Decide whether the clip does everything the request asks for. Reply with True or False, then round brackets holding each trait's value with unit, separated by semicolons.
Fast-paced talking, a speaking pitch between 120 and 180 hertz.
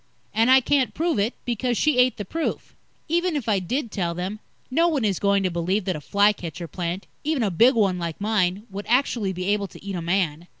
False (230 wpm; 205 Hz)